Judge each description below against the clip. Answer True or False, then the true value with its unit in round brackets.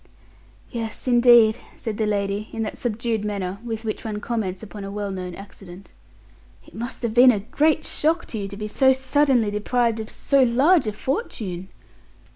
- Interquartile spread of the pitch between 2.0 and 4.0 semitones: True (3.1 semitones)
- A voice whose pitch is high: True (220 Hz)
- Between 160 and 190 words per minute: True (180 wpm)